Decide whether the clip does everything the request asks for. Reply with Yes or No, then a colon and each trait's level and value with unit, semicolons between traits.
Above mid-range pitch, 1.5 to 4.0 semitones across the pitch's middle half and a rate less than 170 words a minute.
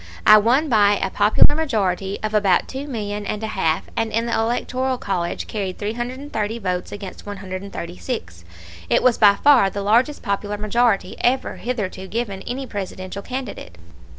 Yes: high, 210 Hz; average, 3.7 semitones; average, 155 wpm